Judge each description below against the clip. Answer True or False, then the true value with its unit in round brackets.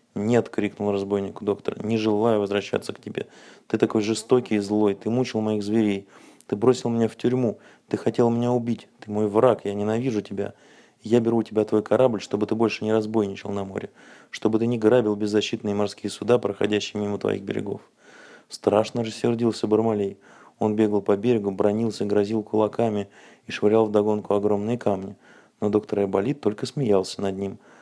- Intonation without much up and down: True (1.8 semitones)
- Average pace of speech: False (175 wpm)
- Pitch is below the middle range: True (105 Hz)